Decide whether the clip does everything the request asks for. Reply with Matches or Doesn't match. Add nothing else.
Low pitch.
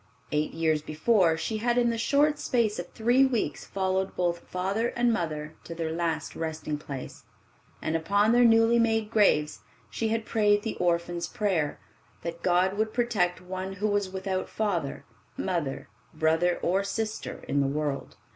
Doesn't match